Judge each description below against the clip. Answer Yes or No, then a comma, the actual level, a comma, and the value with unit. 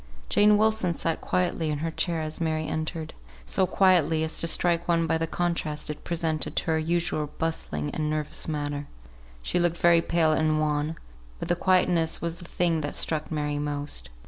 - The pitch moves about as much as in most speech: No, narrow, 2.0 semitones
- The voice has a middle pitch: Yes, medium, 160 Hz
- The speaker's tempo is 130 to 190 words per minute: Yes, average, 185 wpm